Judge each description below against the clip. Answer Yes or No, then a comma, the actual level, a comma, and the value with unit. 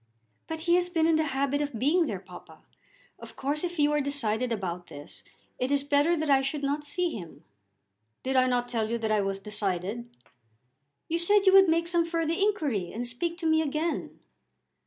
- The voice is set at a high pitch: Yes, very high, 285 Hz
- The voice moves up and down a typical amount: No, wide, 6.1 semitones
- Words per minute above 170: Yes, average, 200 wpm